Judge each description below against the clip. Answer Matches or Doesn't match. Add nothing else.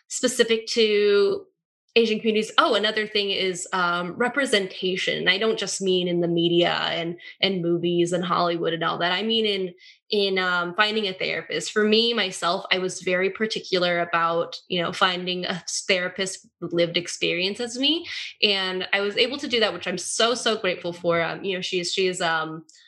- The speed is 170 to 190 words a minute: Matches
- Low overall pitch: Doesn't match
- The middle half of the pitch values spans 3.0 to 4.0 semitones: Matches